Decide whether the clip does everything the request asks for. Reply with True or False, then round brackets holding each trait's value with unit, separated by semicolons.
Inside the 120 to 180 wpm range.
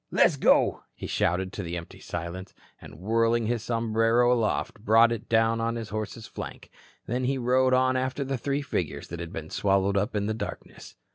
False (195 wpm)